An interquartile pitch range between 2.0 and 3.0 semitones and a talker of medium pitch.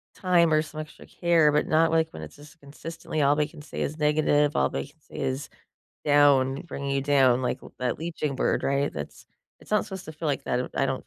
Yes: narrow, 2.4 semitones; medium, 150 Hz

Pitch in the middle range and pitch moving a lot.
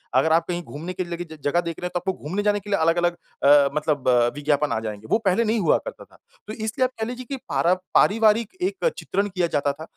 Yes: medium, 175 Hz; wide, 5.8 semitones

